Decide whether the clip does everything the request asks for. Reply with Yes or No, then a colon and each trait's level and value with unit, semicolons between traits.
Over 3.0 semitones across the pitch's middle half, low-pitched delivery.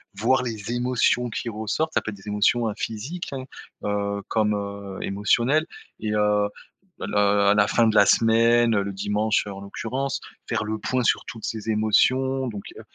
No: average, 2.7 semitones; low, 110 Hz